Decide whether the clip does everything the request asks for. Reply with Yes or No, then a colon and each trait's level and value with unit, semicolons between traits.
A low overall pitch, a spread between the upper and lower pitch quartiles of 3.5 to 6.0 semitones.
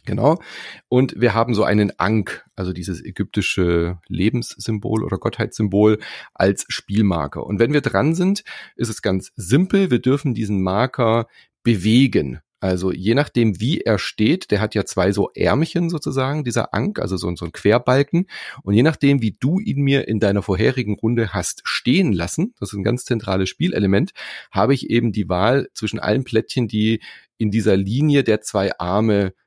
Yes: low, 110 Hz; average, 4.0 semitones